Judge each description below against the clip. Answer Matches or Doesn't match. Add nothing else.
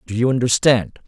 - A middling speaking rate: Matches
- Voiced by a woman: Doesn't match